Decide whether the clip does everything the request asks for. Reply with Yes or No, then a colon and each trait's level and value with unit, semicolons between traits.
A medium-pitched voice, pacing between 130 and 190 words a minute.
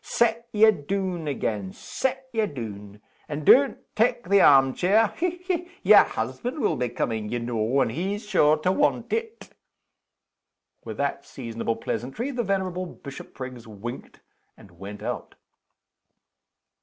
Yes: medium, 155 Hz; average, 140 wpm